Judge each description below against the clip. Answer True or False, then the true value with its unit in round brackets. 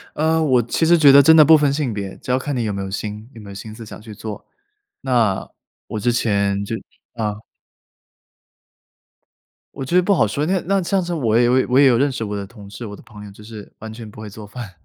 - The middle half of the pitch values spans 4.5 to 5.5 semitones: True (5.2 semitones)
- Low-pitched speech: True (115 Hz)